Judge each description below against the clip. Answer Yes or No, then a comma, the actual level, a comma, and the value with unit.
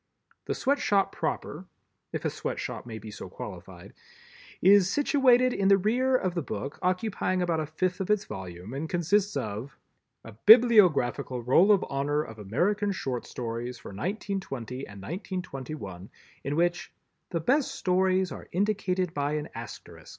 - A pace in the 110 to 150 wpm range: Yes, average, 145 wpm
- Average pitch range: No, wide, 7.9 semitones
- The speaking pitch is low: No, medium, 175 Hz